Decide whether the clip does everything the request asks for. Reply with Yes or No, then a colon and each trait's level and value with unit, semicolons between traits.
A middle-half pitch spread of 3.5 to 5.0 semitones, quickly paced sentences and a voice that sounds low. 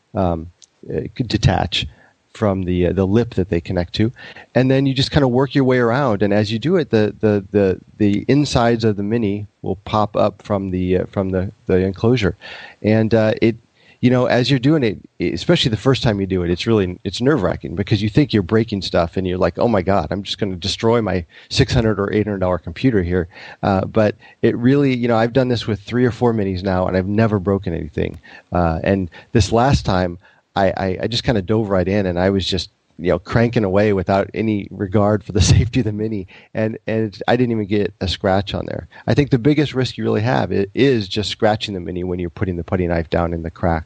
Yes: average, 3.8 semitones; fast, 240 wpm; low, 105 Hz